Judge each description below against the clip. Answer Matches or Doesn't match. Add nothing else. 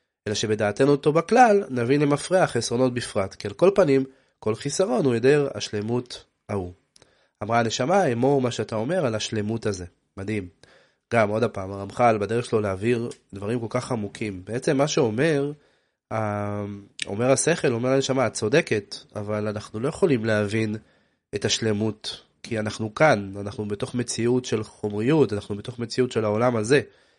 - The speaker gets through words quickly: Matches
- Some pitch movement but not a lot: Matches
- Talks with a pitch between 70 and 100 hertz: Doesn't match